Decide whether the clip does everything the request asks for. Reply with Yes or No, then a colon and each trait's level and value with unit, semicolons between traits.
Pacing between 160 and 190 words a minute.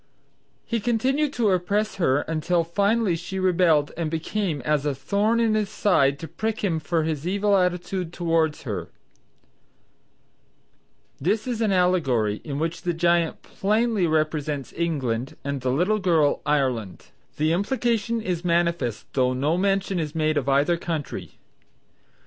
No: average, 145 wpm